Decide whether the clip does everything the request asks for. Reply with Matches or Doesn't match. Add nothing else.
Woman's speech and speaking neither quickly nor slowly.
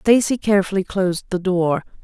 Matches